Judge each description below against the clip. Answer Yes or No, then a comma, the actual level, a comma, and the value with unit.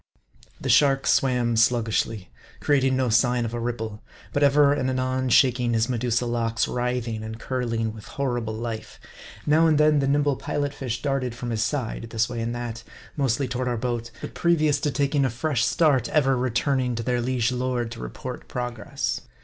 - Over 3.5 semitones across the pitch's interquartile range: No, average, 2.7 semitones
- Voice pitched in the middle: No, low, 125 Hz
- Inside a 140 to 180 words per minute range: No, average, 190 wpm